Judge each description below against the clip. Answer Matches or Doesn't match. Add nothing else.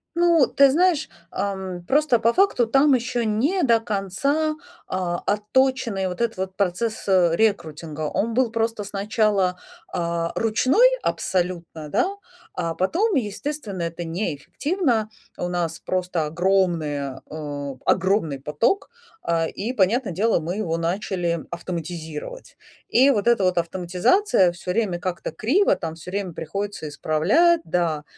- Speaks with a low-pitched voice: Doesn't match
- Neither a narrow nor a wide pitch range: Doesn't match